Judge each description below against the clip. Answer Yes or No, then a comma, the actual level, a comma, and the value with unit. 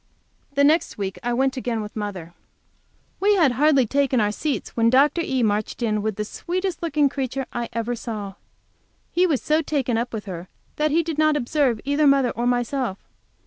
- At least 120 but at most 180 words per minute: No, average, 195 wpm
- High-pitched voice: Yes, very high, 255 Hz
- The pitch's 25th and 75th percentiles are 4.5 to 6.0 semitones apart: Yes, average, 5.0 semitones